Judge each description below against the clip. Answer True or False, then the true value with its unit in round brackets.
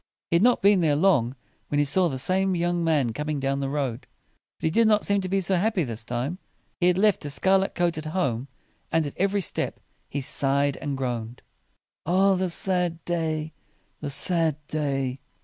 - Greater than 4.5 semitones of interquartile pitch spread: True (5.0 semitones)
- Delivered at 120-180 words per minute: False (200 wpm)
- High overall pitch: False (160 Hz)